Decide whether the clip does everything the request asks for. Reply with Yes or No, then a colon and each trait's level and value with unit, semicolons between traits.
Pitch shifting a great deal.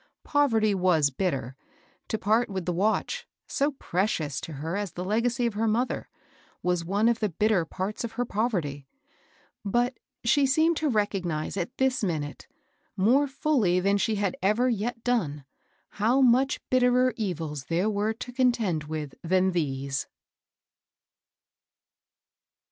Yes: wide, 5.8 semitones